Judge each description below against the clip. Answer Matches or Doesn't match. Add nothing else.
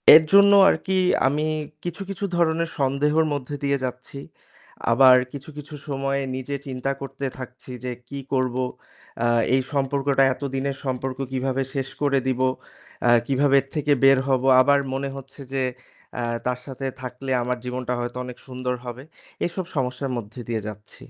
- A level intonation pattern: Matches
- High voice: Doesn't match